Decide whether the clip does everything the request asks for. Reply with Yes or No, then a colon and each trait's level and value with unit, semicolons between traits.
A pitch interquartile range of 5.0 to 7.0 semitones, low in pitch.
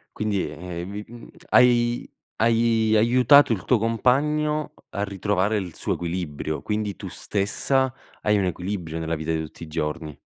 Yes: average, 5.3 semitones; low, 105 Hz